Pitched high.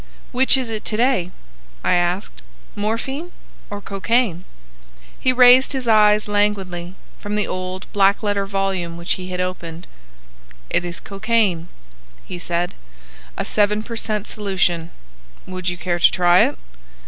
Yes: high, 195 Hz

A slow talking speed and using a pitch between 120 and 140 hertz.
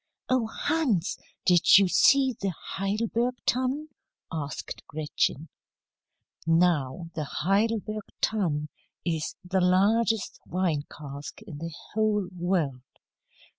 No: slow, 100 wpm; medium, 185 Hz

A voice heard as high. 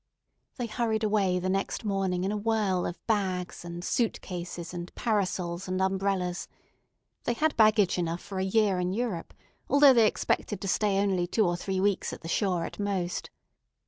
Yes: high, 195 Hz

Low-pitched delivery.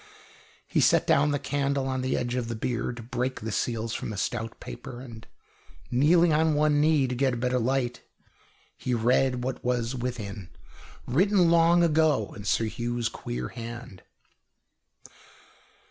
Yes: low, 125 Hz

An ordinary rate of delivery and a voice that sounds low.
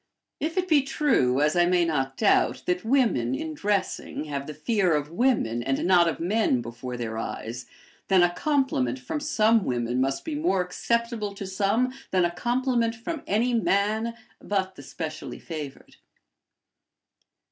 No: average, 160 wpm; medium, 185 Hz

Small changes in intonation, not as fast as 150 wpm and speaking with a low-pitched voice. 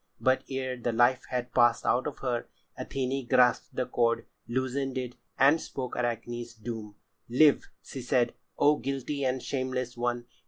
No: narrow, 1.7 semitones; average, 155 wpm; low, 125 Hz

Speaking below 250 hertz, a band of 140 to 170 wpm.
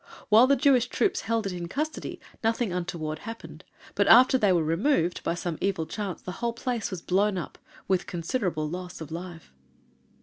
No: high, 190 Hz; average, 180 wpm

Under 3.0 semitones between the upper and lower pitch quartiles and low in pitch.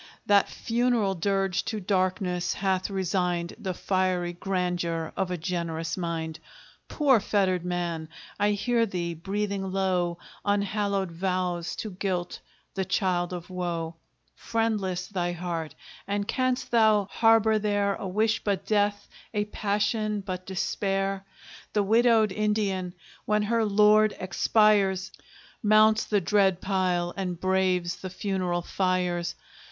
No: narrow, 2.6 semitones; high, 190 Hz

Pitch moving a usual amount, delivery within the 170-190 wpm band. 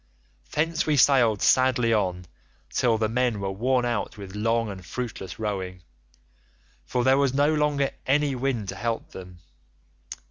No: average, 4.7 semitones; average, 150 wpm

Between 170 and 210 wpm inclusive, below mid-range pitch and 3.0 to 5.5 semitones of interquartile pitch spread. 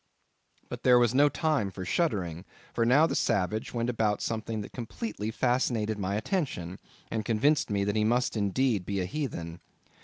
Yes: average, 175 wpm; low, 110 Hz; average, 3.8 semitones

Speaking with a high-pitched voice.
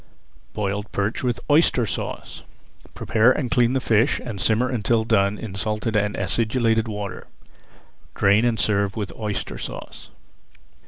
No: low, 110 Hz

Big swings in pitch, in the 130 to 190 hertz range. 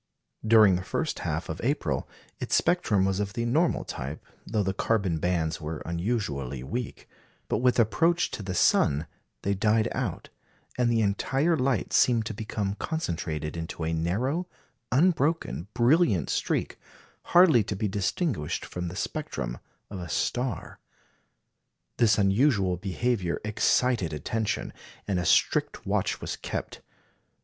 No: wide, 6.1 semitones; low, 105 Hz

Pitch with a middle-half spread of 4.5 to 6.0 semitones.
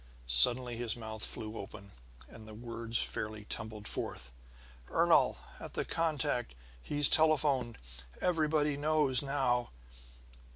Yes: average, 5.1 semitones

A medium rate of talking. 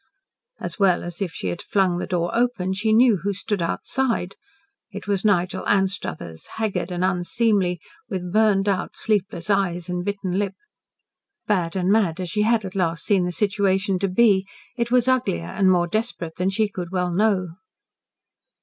Yes: average, 175 wpm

